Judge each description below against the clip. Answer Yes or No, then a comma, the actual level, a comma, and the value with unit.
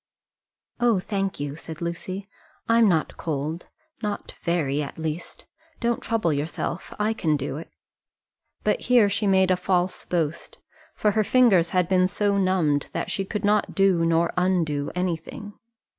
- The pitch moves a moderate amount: Yes, average, 3.9 semitones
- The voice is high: No, medium, 180 Hz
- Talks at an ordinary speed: Yes, average, 160 wpm